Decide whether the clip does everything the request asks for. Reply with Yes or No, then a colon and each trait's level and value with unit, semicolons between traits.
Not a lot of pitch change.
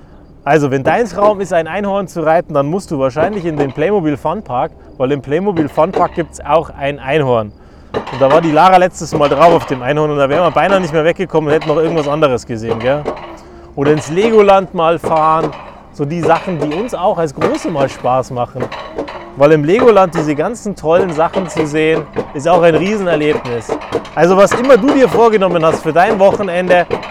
No: average, 3.8 semitones